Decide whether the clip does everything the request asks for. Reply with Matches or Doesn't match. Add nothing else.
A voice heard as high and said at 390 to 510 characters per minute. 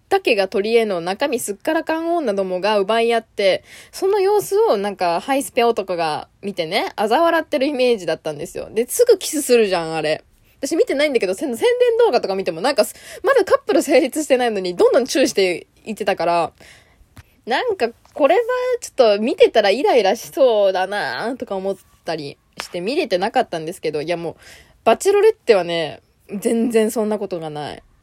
Matches